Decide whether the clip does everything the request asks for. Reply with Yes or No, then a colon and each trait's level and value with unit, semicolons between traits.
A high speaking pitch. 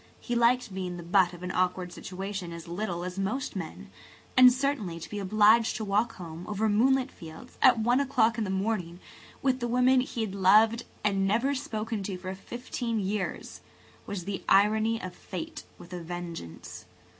Yes: high, 205 Hz